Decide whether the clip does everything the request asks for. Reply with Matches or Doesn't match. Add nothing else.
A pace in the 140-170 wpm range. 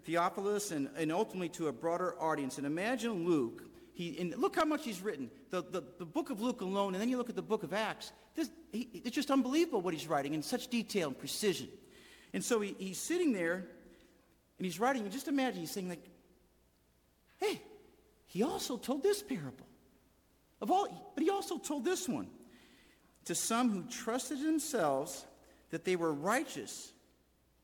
Doesn't match